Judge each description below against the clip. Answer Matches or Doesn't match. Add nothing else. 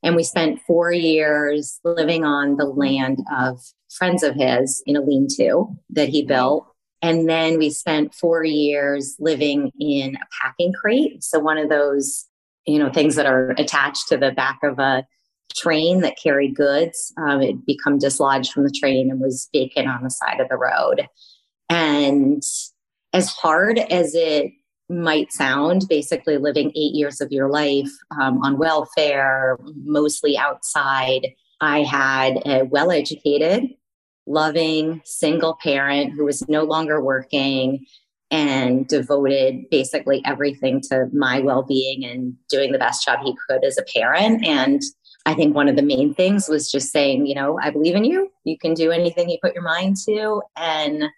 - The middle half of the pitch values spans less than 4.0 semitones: Matches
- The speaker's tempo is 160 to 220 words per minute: Matches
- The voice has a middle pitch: Matches